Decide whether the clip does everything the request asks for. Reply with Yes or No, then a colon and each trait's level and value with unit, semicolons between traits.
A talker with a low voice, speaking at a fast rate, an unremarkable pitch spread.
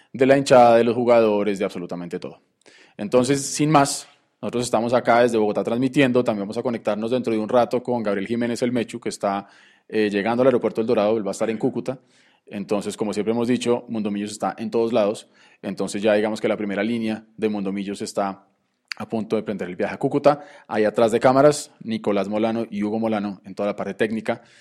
Yes: low, 110 Hz; fast, 210 wpm; average, 3.1 semitones